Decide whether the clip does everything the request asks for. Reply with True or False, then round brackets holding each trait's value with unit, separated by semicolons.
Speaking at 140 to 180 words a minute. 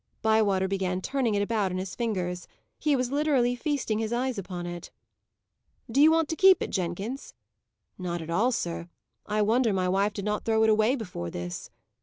False (190 wpm)